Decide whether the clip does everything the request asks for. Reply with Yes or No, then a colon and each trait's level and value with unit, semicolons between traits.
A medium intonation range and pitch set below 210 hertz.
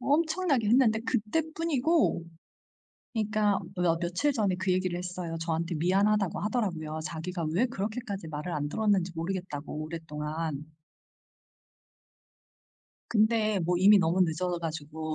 Yes: average, 4.9 semitones; medium, 185 Hz